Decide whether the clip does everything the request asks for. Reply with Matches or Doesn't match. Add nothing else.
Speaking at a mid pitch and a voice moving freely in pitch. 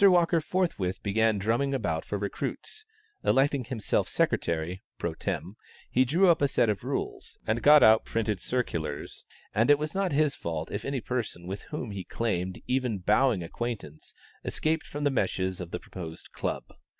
Doesn't match